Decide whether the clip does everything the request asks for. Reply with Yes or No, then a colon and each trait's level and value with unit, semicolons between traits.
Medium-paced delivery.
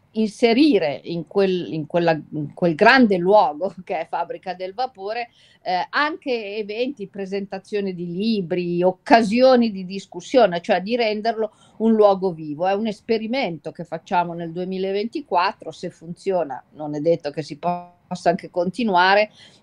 Yes: average, 140 wpm